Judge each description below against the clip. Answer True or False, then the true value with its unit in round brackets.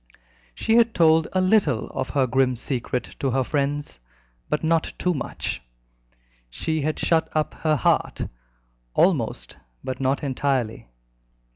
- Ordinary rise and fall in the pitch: True (3.6 semitones)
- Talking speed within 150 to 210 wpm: False (135 wpm)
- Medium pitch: True (145 Hz)